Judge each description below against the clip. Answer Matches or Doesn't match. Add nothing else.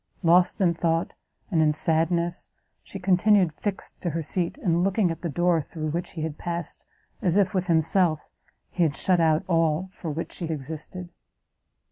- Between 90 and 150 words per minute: Doesn't match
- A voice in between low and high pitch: Matches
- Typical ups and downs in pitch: Doesn't match